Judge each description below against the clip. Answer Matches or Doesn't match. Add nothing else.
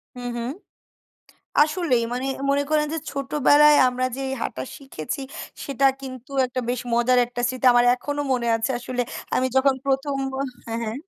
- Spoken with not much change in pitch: Matches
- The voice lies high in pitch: Matches